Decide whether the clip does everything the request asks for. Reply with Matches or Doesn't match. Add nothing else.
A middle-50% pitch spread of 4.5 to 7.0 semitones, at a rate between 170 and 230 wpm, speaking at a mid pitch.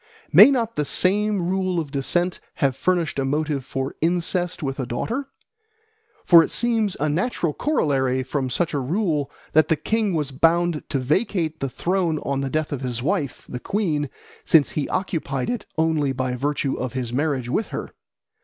Matches